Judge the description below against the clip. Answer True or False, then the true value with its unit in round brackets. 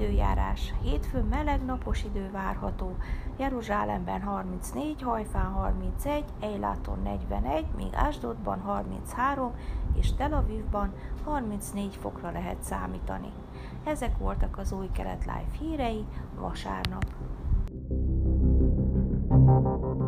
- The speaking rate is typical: False (90 wpm)